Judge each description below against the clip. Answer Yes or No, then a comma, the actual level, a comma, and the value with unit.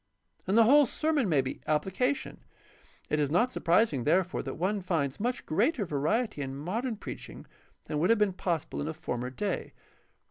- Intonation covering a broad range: Yes, wide, 7.3 semitones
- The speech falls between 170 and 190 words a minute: Yes, average, 180 wpm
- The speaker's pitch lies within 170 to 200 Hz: Yes, medium, 185 Hz